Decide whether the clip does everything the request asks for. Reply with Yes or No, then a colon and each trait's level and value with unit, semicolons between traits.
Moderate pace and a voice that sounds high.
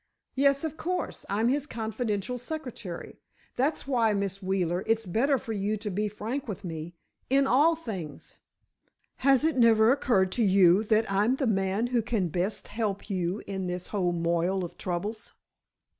Yes: average, 160 wpm; high, 215 Hz